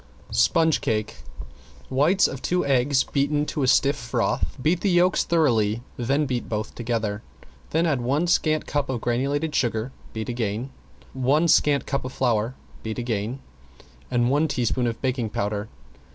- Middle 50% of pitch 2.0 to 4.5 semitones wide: Yes, average, 4.2 semitones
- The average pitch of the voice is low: Yes, low, 130 Hz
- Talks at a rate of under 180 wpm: Yes, average, 155 wpm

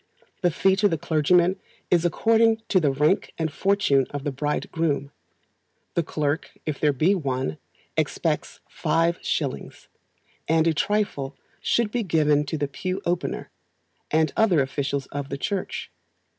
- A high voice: No, medium, 160 Hz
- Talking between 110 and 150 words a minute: Yes, average, 145 wpm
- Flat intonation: No, average, 4.4 semitones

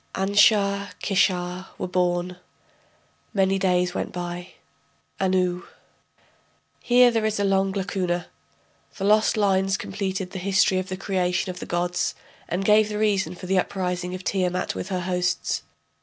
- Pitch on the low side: No, high, 190 Hz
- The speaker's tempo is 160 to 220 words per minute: No, average, 145 wpm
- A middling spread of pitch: No, narrow, 1.7 semitones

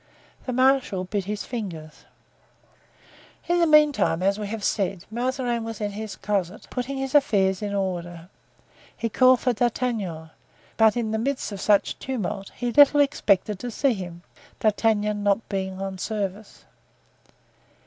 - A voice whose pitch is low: No, high, 210 Hz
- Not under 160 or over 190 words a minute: No, average, 150 wpm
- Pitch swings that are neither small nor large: Yes, average, 4.2 semitones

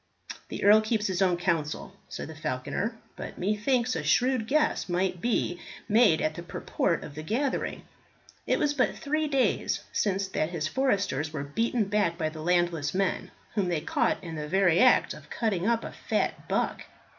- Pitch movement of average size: No, wide, 5.7 semitones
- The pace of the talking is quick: No, average, 180 wpm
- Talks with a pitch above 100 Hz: Yes, high, 190 Hz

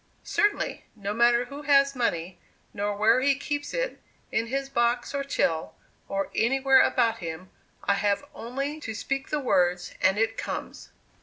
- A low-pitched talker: No, high, 235 Hz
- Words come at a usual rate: Yes, average, 160 wpm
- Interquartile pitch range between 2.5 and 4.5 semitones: No, wide, 5.4 semitones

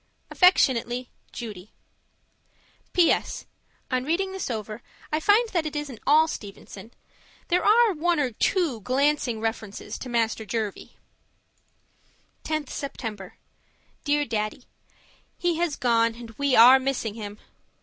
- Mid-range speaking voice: No, very high, 255 Hz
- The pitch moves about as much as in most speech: No, wide, 5.8 semitones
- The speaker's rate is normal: No, slow, 120 wpm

